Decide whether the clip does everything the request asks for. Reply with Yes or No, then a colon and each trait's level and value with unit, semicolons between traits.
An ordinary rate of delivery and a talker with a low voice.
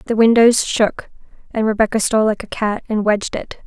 No: average, 195 wpm; high, 220 Hz